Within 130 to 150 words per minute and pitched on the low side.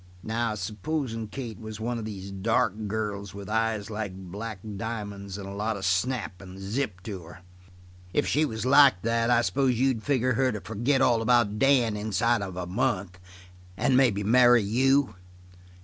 No: average, 175 wpm; low, 110 Hz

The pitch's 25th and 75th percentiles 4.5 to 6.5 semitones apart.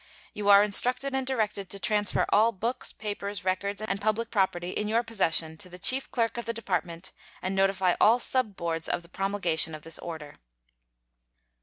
No: average, 3.8 semitones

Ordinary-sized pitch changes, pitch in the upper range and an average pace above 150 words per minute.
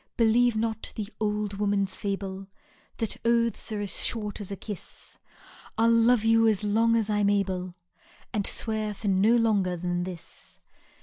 No: narrow, 2.3 semitones; high, 210 Hz; average, 170 wpm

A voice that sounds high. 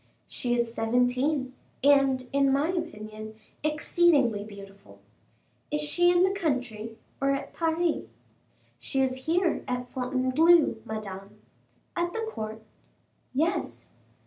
Yes: very high, 265 Hz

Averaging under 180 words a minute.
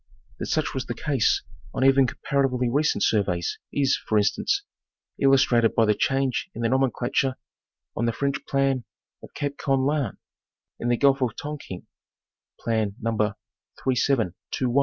Yes: average, 140 wpm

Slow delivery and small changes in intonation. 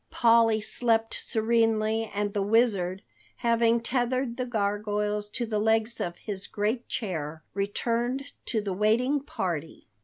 Yes: slow, 130 wpm; narrow, 2.3 semitones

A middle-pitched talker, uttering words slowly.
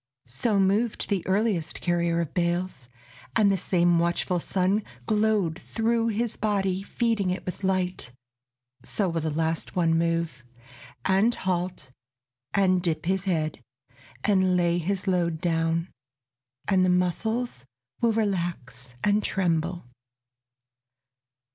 Yes: medium, 180 Hz; slow, 125 wpm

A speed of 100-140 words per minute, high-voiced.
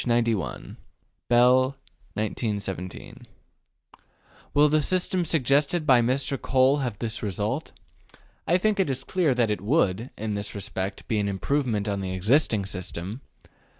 No: slow, 135 wpm; low, 120 Hz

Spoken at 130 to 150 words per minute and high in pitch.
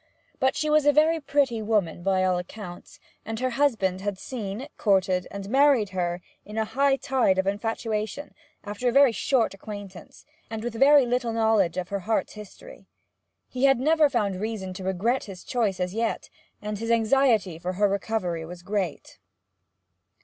No: average, 170 wpm; high, 215 Hz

